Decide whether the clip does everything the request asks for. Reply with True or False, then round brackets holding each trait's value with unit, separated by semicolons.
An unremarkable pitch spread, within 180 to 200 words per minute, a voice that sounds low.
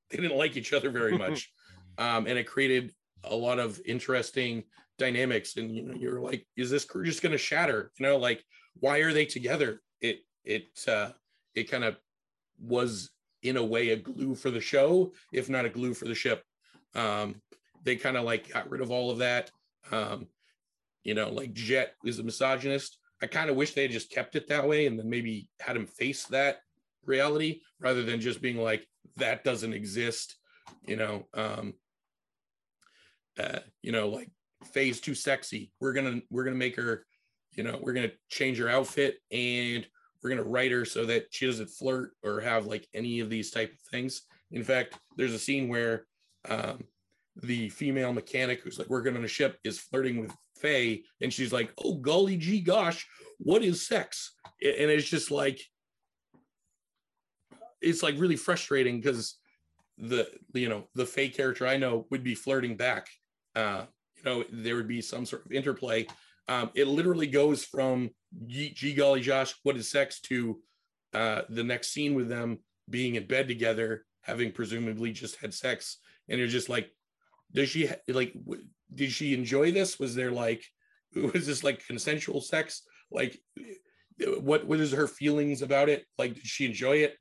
True (3.4 semitones; 185 wpm; 130 Hz)